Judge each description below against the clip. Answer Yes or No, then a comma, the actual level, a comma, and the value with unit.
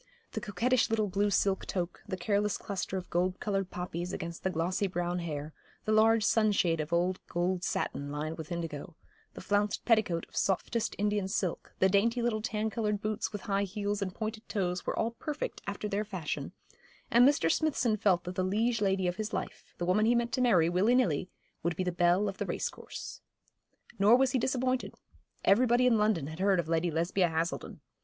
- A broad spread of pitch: No, average, 3.7 semitones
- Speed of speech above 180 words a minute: Yes, average, 200 wpm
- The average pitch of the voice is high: Yes, high, 195 Hz